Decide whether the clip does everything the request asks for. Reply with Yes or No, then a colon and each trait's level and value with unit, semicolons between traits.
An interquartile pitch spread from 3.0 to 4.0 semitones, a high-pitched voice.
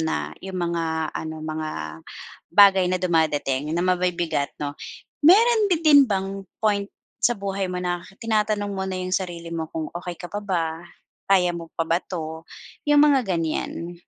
No: average, 3.5 semitones; medium, 180 Hz